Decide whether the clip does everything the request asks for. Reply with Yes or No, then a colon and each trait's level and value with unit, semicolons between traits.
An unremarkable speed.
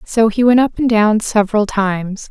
No: fast, 210 wpm